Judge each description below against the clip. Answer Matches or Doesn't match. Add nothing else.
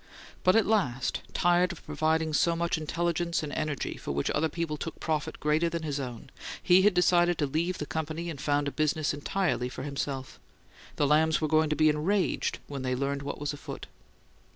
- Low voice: Doesn't match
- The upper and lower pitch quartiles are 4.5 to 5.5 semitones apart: Doesn't match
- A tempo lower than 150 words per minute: Doesn't match